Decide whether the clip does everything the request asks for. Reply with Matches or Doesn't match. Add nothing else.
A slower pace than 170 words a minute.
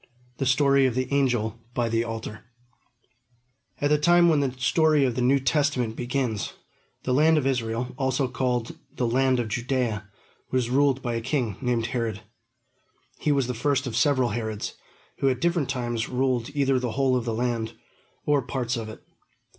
Doesn't match